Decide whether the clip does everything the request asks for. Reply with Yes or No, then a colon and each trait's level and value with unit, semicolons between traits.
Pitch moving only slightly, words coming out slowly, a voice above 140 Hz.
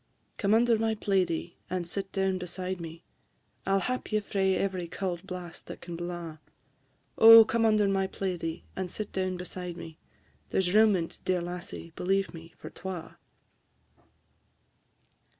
No: narrow, 2.2 semitones; average, 160 wpm; medium, 185 Hz